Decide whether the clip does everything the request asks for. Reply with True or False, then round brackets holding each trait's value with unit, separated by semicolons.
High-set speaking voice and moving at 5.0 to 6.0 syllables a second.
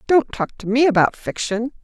True (240 Hz; 5.3 syllables/s)